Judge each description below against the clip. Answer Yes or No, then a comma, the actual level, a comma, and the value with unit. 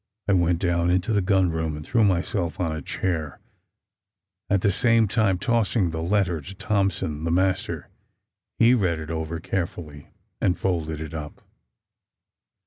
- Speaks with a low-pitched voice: Yes, very low, 90 Hz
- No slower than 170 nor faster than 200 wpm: No, average, 155 wpm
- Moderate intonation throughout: Yes, average, 3.5 semitones